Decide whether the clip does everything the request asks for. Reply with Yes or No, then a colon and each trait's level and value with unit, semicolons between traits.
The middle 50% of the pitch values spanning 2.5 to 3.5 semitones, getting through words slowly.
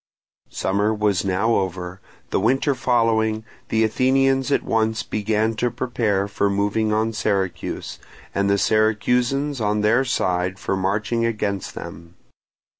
Yes: average, 2.8 semitones; slow, 130 wpm